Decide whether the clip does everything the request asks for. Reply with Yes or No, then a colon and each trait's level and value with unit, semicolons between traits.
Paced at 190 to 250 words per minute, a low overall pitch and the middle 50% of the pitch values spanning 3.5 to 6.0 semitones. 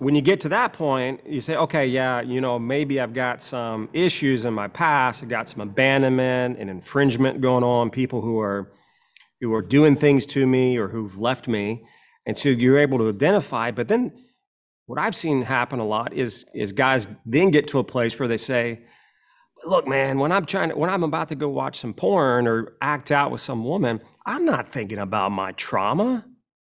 Yes: fast, 205 wpm; low, 130 Hz; average, 3.8 semitones